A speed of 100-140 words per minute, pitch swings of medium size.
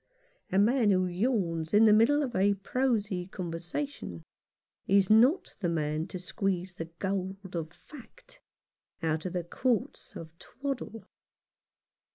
Yes: slow, 135 wpm; average, 4.8 semitones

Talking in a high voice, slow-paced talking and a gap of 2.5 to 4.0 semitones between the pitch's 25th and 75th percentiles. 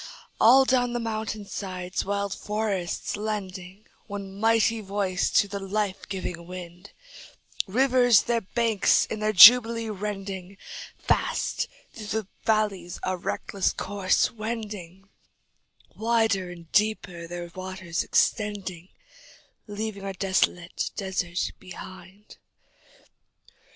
Yes: high, 200 Hz; slow, 105 wpm; average, 2.8 semitones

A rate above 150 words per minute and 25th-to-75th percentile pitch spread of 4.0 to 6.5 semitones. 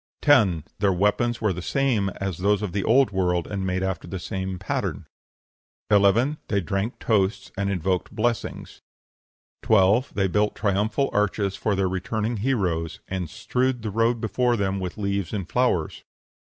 No: average, 160 wpm; average, 3.0 semitones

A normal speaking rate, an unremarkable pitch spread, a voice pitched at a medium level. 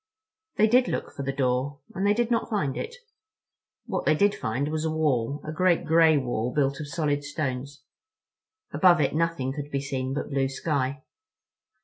Yes: average, 170 wpm; average, 3.7 semitones; medium, 145 Hz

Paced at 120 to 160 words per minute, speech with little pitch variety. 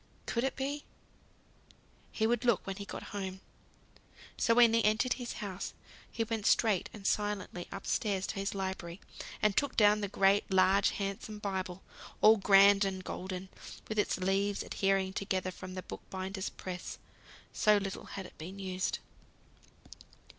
Yes: average, 155 wpm; narrow, 2.0 semitones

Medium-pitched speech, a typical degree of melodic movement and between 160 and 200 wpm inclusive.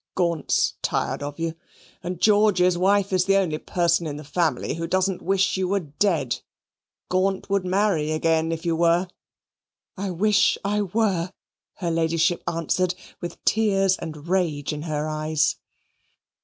No: medium, 175 Hz; average, 3.1 semitones; average, 150 wpm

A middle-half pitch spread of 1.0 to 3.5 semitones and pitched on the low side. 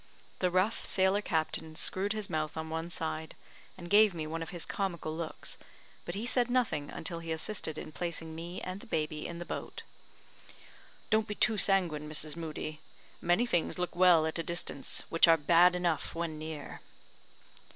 No: average, 2.8 semitones; medium, 170 Hz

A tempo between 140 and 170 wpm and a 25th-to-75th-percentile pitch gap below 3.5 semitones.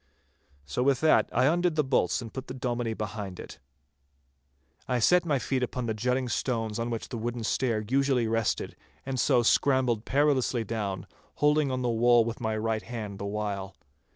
No: average, 185 wpm; average, 3.0 semitones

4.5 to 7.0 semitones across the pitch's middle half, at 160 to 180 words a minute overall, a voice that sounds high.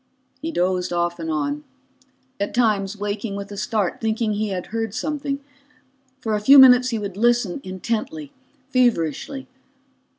No: average, 4.8 semitones; average, 145 wpm; high, 215 Hz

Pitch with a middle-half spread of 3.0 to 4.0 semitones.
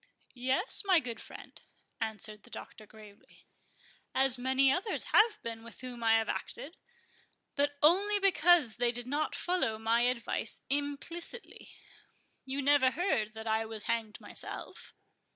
No: average, 5.3 semitones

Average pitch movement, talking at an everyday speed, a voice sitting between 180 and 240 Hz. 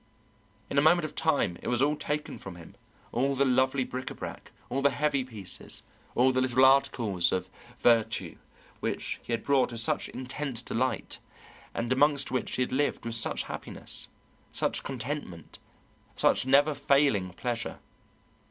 No: average, 3.3 semitones; average, 160 wpm; low, 130 Hz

